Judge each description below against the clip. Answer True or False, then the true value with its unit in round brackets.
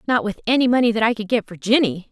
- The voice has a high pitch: True (220 Hz)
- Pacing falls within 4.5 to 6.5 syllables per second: False (6.9 syllables/s)